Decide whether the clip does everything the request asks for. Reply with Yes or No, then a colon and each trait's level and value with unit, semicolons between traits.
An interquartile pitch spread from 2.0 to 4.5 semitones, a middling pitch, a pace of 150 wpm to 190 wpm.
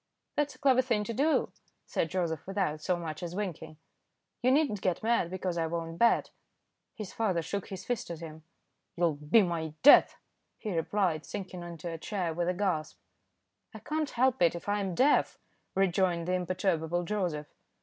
Yes: average, 3.9 semitones; medium, 180 Hz; average, 180 wpm